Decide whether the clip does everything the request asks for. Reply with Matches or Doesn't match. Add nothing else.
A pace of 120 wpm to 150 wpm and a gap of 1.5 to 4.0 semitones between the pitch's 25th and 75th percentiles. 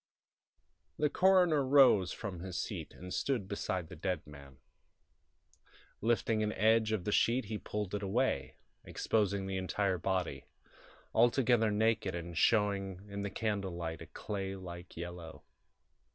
Matches